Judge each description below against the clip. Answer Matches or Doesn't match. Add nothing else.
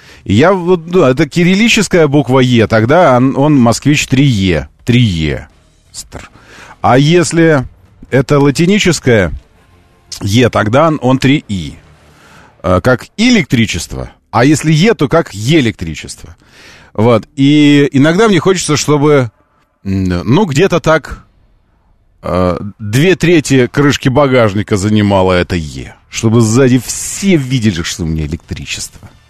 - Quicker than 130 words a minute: Doesn't match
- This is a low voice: Matches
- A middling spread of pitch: Doesn't match